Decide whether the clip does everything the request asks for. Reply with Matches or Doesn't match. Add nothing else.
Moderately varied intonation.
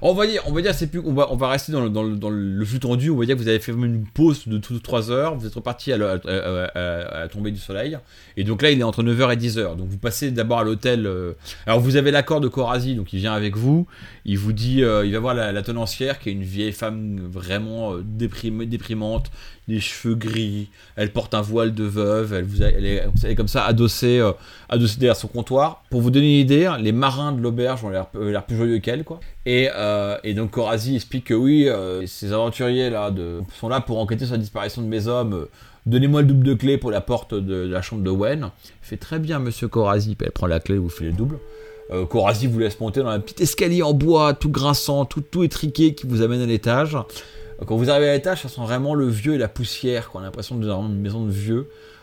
Matches